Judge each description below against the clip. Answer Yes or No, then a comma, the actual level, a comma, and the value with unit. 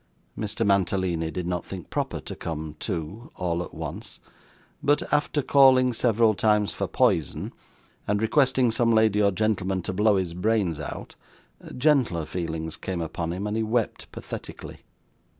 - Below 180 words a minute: Yes, average, 150 wpm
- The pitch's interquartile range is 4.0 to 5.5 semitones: Yes, average, 4.5 semitones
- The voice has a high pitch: No, low, 100 Hz